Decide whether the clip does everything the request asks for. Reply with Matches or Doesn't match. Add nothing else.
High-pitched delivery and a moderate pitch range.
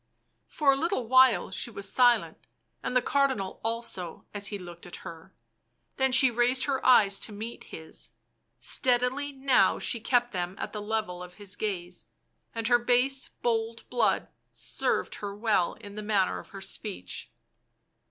Matches